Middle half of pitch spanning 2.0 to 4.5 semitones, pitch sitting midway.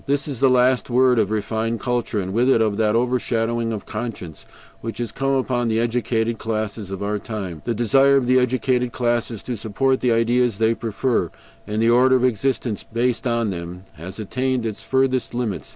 No: narrow, 2.5 semitones; low, 115 Hz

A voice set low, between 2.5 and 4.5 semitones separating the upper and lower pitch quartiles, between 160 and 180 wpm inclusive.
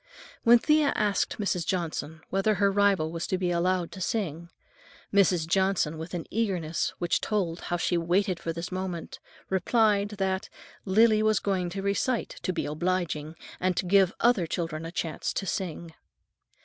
No: medium, 185 Hz; average, 2.9 semitones; average, 170 wpm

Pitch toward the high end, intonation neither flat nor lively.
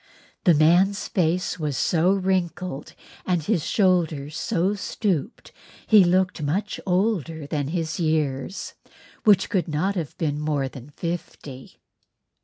No: medium, 170 Hz; average, 3.8 semitones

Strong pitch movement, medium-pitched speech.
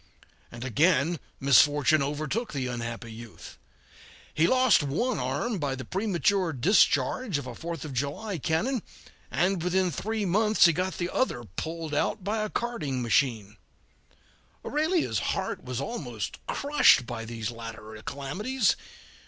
Yes: wide, 8.3 semitones; medium, 160 Hz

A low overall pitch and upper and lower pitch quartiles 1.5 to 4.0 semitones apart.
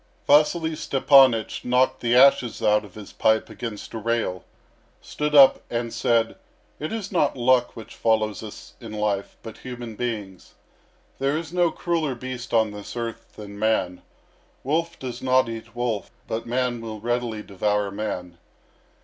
Yes: low, 115 Hz; average, 3.3 semitones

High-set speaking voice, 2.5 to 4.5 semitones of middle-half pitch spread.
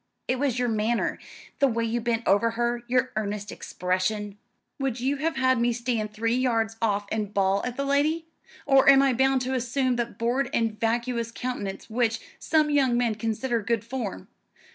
Yes: high, 235 Hz; average, 2.8 semitones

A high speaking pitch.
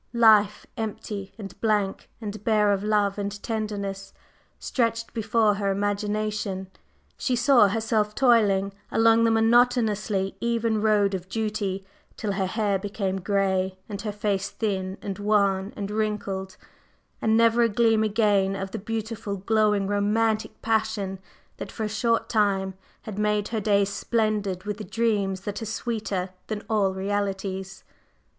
Yes: high, 210 Hz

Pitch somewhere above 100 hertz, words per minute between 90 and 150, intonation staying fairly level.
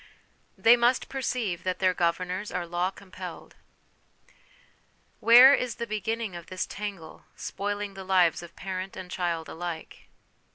No: medium, 185 Hz; slow, 135 wpm; average, 3.4 semitones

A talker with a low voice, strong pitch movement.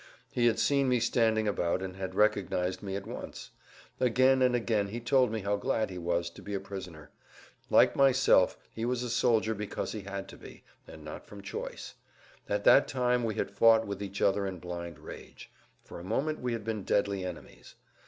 No: low, 105 Hz; average, 3.9 semitones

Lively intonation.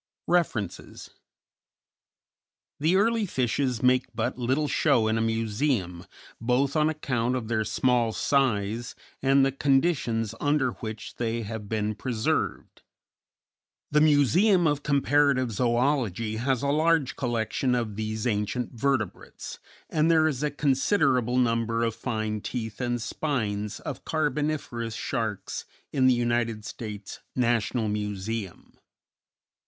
No: average, 4.0 semitones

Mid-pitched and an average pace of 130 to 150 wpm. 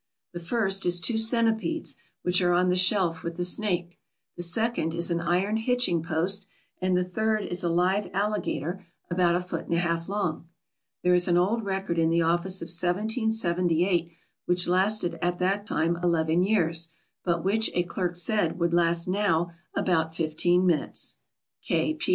No: medium, 180 Hz; average, 170 wpm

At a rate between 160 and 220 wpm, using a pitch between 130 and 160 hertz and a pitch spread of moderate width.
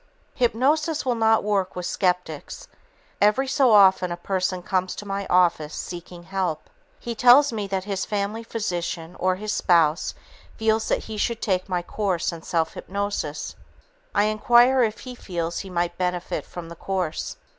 No: average, 165 wpm; high, 195 Hz; average, 3.8 semitones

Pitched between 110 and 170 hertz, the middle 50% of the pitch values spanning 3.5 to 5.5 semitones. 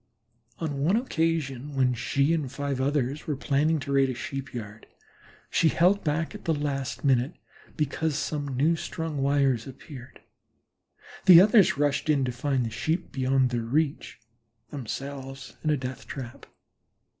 No: medium, 140 Hz; average, 2.8 semitones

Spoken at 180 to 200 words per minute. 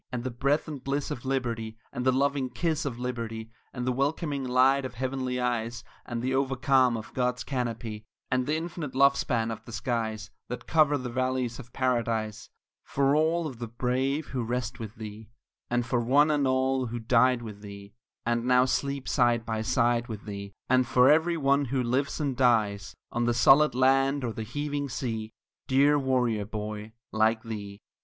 Yes: average, 190 wpm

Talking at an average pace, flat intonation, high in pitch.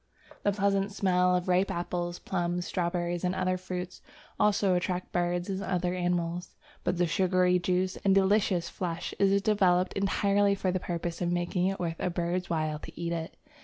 No: average, 175 wpm; narrow, 1.5 semitones; medium, 180 Hz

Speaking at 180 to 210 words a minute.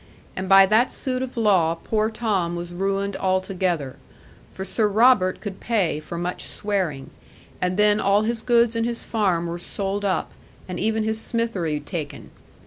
No: average, 165 wpm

